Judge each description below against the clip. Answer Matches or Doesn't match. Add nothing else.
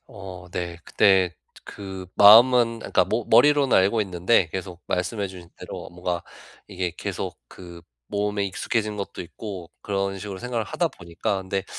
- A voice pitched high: Doesn't match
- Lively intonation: Doesn't match